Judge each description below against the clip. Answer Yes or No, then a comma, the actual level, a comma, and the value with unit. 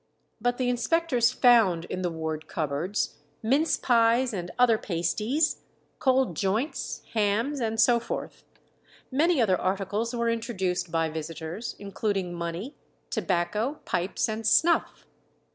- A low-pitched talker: No, high, 220 Hz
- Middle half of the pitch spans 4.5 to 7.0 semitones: Yes, wide, 5.5 semitones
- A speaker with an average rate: No, slow, 125 wpm